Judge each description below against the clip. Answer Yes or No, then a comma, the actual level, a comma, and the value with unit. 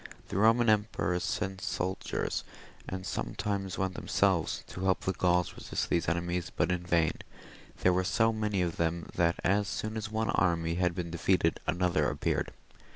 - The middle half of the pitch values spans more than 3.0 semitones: No, average, 2.7 semitones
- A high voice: No, very low, 90 Hz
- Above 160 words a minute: Yes, average, 170 wpm